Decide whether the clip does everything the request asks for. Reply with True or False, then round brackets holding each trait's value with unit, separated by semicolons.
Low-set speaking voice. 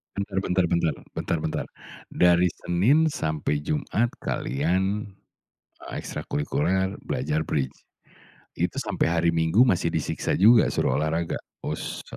True (85 Hz)